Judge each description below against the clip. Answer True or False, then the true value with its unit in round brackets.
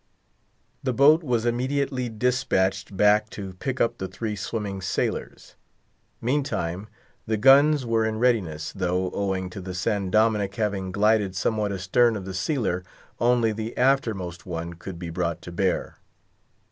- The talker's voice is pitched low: True (105 Hz)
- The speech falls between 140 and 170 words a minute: True (145 wpm)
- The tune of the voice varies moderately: True (4.3 semitones)